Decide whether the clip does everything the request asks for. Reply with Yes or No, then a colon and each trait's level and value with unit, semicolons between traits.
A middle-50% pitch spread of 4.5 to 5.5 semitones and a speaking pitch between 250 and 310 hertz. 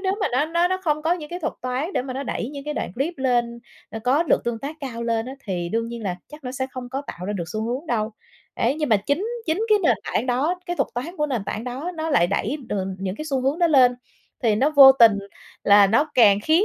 Yes: average, 5.0 semitones; very high, 260 Hz